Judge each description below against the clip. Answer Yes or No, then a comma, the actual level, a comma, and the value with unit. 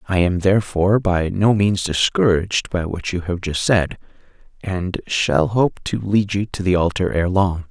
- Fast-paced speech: No, average, 185 wpm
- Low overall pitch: Yes, very low, 95 Hz